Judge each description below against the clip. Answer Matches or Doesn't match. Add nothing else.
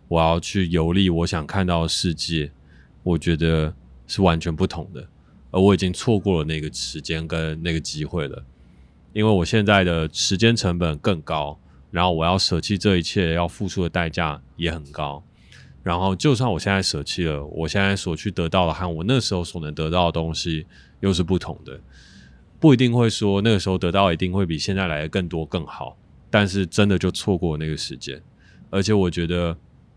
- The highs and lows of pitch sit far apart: Doesn't match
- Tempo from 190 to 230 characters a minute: Doesn't match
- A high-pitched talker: Doesn't match